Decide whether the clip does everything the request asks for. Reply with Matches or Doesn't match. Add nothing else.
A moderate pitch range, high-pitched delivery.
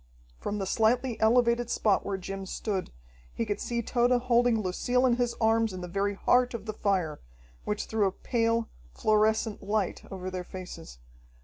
Matches